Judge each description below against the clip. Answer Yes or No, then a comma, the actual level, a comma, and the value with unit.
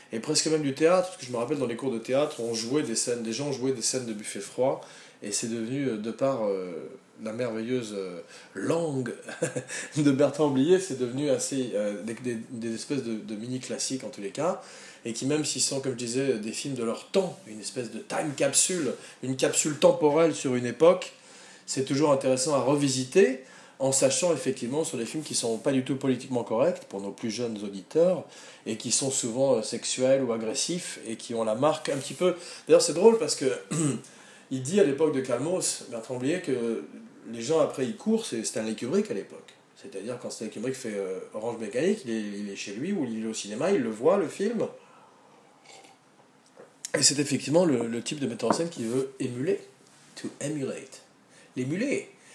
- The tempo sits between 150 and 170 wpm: No, average, 205 wpm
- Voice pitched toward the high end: No, low, 130 Hz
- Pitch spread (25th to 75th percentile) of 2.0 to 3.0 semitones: No, average, 4.8 semitones